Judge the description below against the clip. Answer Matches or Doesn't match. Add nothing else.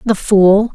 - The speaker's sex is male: Doesn't match